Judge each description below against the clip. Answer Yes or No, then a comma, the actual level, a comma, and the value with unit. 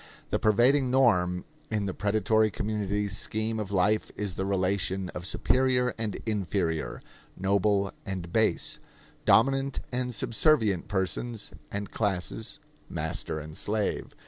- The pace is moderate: No, slow, 120 wpm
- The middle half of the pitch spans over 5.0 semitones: No, average, 2.9 semitones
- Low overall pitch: Yes, low, 105 Hz